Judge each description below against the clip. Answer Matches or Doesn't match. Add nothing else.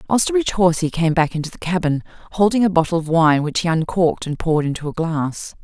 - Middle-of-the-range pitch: Matches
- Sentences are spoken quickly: Matches